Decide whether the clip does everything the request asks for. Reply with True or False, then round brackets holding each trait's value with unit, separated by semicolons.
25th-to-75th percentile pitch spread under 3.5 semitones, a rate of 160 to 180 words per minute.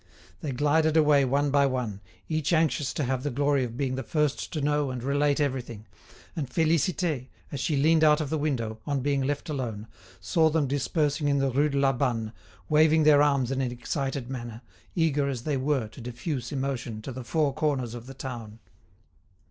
False (2.9 semitones; 195 wpm)